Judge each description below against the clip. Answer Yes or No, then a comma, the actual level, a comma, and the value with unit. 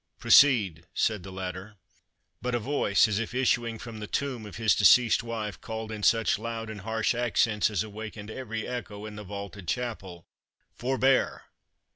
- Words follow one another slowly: No, average, 165 wpm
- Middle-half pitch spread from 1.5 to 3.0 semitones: Yes, narrow, 2.4 semitones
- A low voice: Yes, low, 110 Hz